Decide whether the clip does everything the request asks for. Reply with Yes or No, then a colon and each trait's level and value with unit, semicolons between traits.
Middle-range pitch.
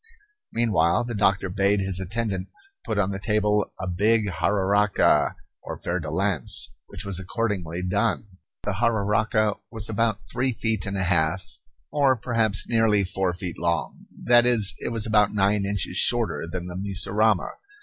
No: low, 100 Hz